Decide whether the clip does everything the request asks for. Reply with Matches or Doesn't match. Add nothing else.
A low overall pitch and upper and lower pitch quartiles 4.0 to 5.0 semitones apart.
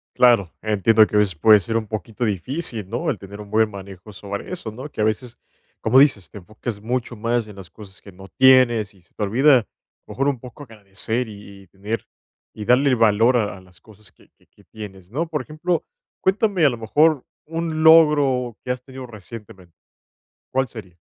Matches